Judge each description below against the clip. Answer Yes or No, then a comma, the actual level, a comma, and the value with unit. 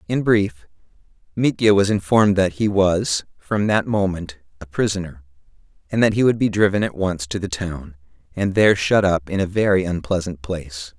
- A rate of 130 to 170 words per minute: No, average, 180 wpm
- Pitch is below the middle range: Yes, very low, 95 Hz